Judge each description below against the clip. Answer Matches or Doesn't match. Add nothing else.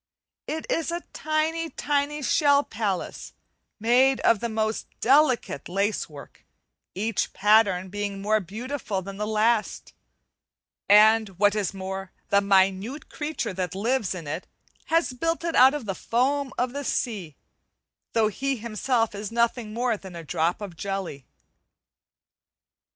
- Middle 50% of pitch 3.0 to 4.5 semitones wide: Doesn't match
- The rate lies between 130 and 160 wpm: Matches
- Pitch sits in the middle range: Doesn't match